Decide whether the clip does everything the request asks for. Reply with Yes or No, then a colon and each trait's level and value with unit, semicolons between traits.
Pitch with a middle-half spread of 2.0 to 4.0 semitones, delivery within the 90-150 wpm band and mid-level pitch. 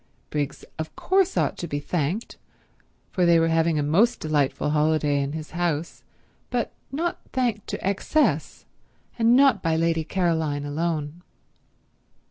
No: average, 4.5 semitones; average, 140 wpm; medium, 165 Hz